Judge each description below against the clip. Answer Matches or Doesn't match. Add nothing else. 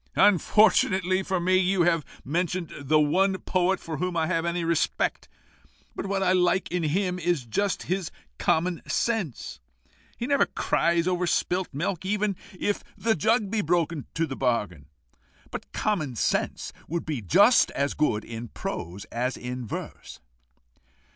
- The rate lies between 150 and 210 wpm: Matches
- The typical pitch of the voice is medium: Matches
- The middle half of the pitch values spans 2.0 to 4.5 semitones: Matches